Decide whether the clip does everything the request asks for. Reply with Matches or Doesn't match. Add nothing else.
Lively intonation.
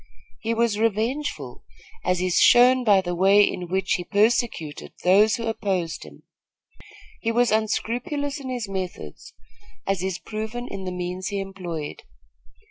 Doesn't match